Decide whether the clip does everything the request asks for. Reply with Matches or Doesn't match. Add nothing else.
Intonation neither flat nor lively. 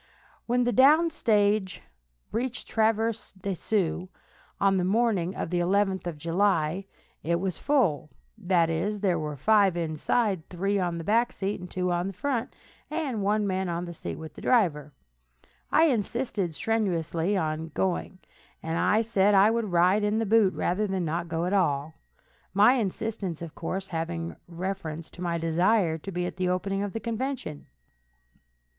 Matches